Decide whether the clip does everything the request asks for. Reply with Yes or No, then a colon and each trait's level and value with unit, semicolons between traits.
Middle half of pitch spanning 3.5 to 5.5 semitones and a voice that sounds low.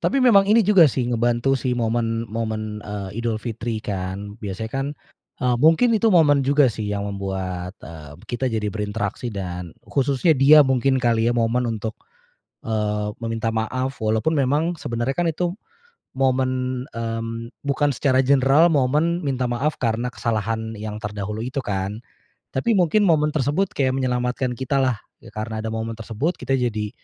Yes: average, 3.9 semitones; low, 120 Hz